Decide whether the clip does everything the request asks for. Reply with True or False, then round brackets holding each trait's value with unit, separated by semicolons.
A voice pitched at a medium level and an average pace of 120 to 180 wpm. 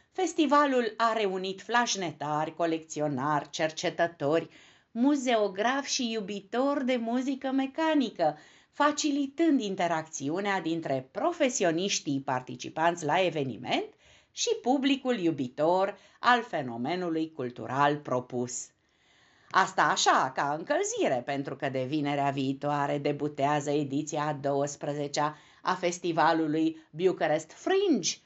False (165 Hz; 90 wpm)